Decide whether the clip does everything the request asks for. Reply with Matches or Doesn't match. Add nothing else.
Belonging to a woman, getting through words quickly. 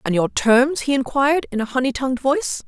Matches